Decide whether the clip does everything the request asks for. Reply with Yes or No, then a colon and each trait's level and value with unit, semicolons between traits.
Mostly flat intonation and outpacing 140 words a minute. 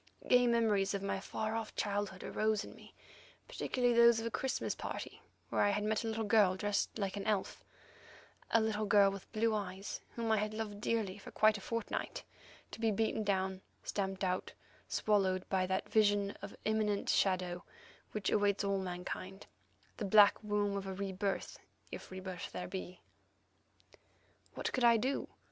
Yes: narrow, 2.1 semitones; average, 180 wpm